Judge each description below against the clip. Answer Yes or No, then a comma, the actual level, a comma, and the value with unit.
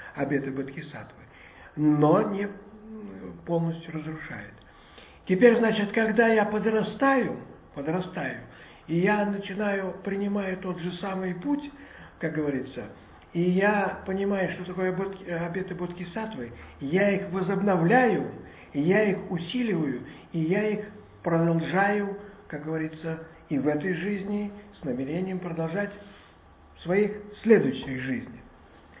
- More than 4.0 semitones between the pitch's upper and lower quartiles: Yes, average, 4.4 semitones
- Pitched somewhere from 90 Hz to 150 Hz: No, medium, 185 Hz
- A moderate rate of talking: No, slow, 110 wpm